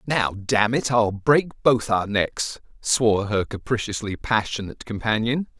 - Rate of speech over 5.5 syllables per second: No, 4.3 syllables/s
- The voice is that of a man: Yes, male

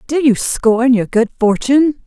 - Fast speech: No, average, 175 wpm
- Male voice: No, female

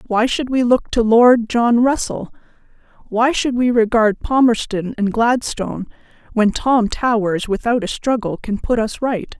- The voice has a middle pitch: No, high, 230 Hz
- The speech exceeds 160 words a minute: No, average, 155 wpm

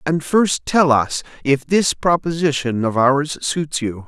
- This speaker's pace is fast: No, average, 160 wpm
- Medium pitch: Yes, medium, 145 Hz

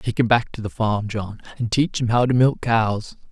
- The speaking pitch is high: No, low, 115 Hz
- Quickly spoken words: Yes, fast, 255 wpm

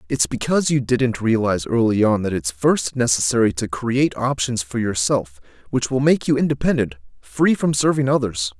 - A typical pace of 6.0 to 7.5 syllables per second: No, 5.2 syllables/s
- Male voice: Yes, male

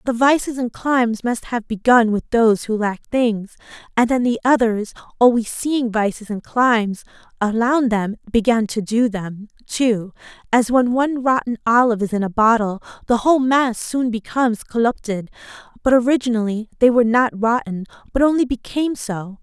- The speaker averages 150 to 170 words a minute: Yes, average, 160 wpm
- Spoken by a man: No, female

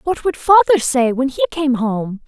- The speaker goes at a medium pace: No, fast, 210 wpm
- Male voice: No, female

